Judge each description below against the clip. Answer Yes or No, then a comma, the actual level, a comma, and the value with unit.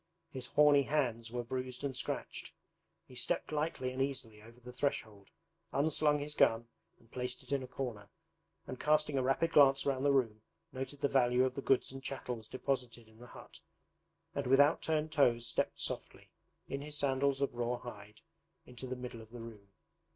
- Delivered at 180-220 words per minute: Yes, average, 190 wpm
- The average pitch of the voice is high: No, low, 130 Hz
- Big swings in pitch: No, average, 2.8 semitones